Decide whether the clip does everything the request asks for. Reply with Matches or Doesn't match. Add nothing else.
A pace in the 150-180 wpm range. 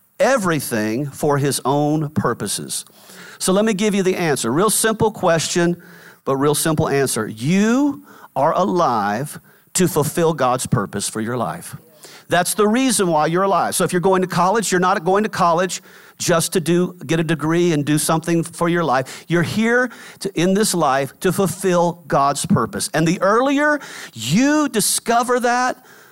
Matches